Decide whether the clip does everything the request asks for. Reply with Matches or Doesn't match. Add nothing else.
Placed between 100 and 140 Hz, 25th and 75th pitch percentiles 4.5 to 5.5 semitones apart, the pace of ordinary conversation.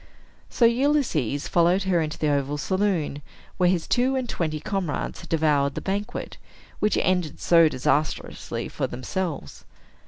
Doesn't match